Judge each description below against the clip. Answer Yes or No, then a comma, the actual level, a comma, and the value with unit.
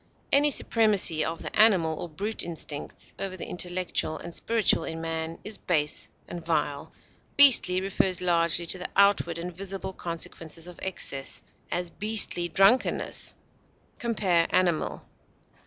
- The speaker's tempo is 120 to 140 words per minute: Yes, slow, 135 wpm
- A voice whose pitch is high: No, medium, 175 Hz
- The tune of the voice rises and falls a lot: No, average, 3.0 semitones